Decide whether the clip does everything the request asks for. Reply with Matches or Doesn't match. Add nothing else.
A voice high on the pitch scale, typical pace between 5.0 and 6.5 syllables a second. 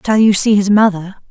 Matches